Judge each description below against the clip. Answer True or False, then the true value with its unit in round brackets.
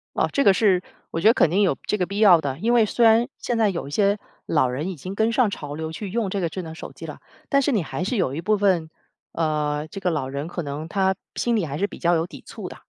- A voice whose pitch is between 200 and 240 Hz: False (185 Hz)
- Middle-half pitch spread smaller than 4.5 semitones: False (5.0 semitones)